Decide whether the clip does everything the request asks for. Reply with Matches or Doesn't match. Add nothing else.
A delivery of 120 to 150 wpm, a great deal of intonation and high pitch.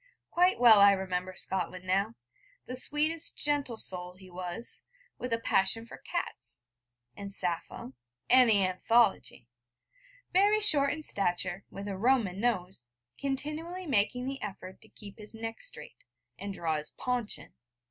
Matches